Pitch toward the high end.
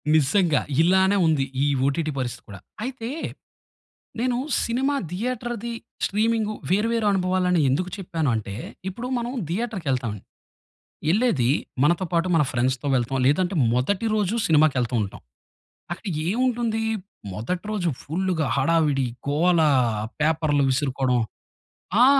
No: medium, 175 Hz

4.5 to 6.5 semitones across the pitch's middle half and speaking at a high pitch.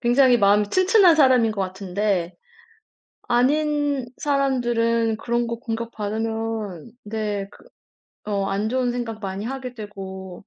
No: average, 3.6 semitones; high, 225 Hz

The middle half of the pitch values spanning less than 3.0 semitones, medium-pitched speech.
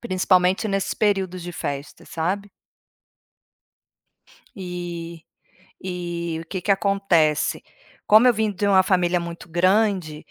Yes: narrow, 2.6 semitones; medium, 180 Hz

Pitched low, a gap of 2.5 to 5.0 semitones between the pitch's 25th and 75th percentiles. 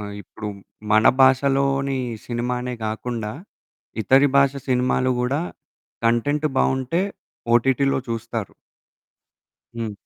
Yes: low, 125 Hz; average, 2.9 semitones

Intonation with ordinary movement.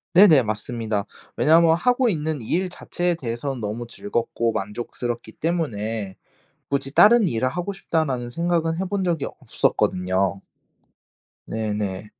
No: wide, 7.7 semitones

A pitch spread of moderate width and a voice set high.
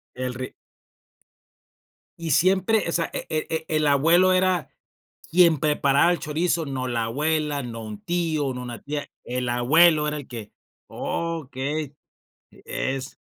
No: average, 4.5 semitones; medium, 150 Hz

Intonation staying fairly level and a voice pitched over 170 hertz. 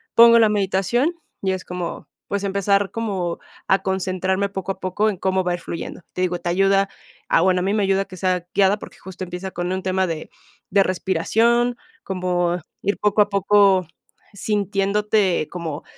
Yes: narrow, 1.8 semitones; high, 190 Hz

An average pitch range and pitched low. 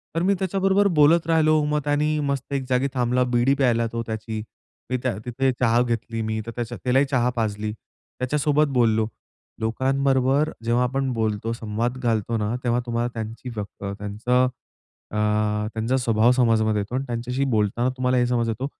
Yes: average, 3.1 semitones; low, 120 Hz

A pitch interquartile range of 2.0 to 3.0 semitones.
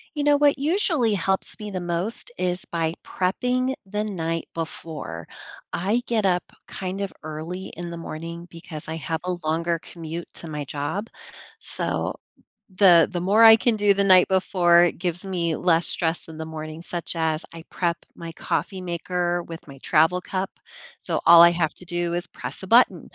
Yes: average, 2.7 semitones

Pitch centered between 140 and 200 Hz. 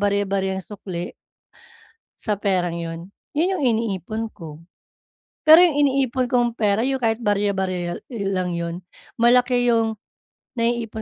No: high, 215 Hz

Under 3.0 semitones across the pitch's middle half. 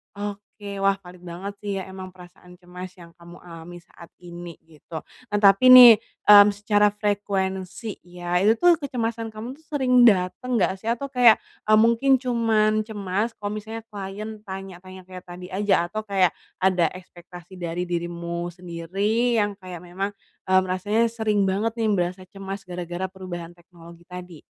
No: average, 3.3 semitones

